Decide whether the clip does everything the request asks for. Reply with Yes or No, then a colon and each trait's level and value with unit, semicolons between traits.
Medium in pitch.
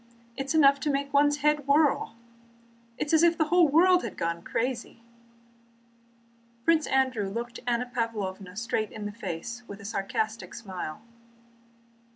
No: high, 245 Hz